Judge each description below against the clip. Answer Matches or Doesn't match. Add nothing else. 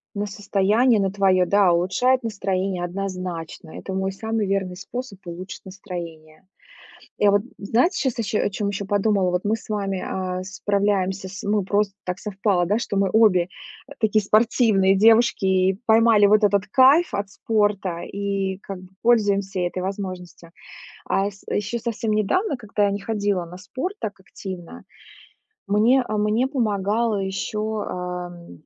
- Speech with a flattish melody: Matches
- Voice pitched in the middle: Doesn't match